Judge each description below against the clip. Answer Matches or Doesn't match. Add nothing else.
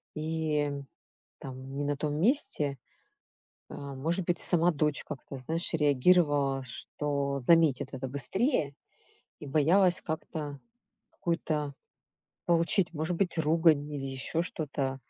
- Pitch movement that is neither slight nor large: Matches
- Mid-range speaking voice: Matches